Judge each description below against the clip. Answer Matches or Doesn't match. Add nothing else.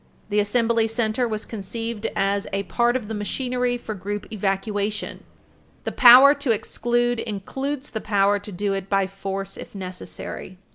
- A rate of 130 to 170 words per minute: Matches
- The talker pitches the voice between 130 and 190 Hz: Doesn't match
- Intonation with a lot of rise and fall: Doesn't match